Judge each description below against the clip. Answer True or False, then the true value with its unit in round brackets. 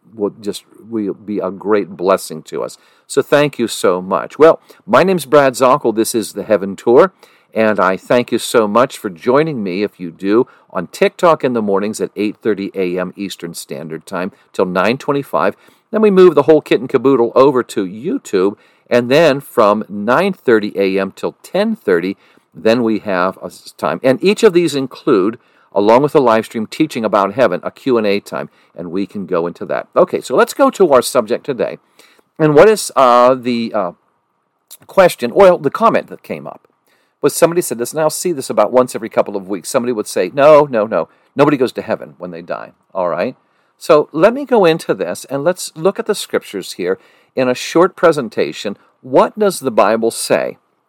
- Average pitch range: False (8.3 semitones)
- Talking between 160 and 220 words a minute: True (195 wpm)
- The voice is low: True (125 Hz)